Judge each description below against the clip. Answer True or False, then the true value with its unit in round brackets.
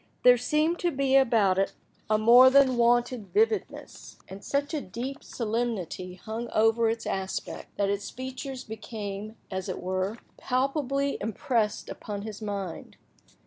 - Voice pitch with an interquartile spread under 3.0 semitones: False (4.4 semitones)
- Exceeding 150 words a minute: False (145 wpm)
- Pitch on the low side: False (230 Hz)